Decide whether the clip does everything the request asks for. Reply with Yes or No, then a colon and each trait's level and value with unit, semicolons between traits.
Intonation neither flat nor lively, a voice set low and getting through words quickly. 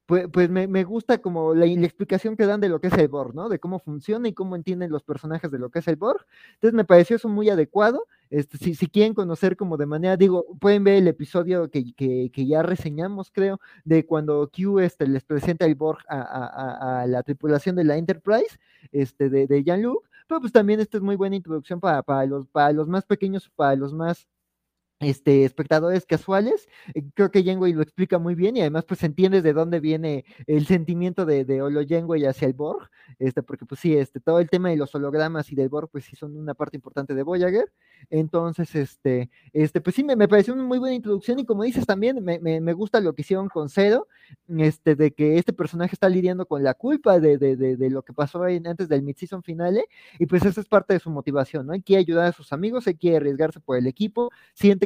No: average, 4.7 semitones; medium, 170 Hz; fast, 230 wpm